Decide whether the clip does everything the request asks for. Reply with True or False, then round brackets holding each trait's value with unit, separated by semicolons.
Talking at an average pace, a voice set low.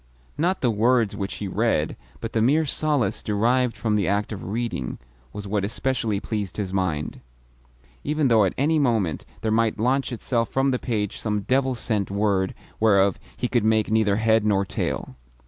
True (180 wpm; 110 Hz)